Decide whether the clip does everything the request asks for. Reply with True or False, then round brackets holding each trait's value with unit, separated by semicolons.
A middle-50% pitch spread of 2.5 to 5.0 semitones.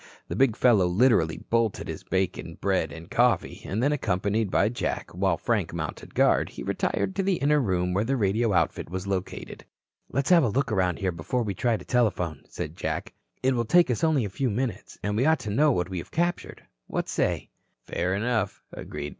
False (5.6 semitones)